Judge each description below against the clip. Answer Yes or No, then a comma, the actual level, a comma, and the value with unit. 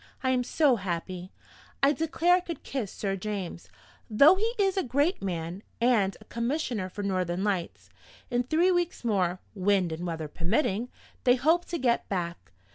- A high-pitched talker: Yes, high, 215 Hz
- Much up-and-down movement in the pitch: Yes, wide, 7.8 semitones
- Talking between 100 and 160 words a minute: No, average, 170 wpm